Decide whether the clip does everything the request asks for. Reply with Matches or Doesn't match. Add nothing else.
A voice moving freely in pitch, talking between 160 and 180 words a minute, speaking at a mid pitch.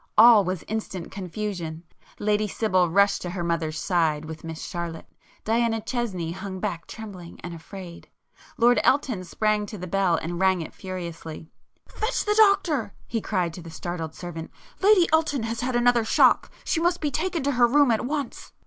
Doesn't match